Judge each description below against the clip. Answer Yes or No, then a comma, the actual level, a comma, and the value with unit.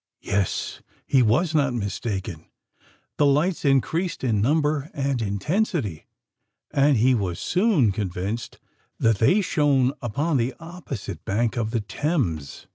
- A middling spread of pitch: No, wide, 6.4 semitones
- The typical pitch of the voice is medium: No, low, 130 Hz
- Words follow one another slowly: Yes, slow, 125 wpm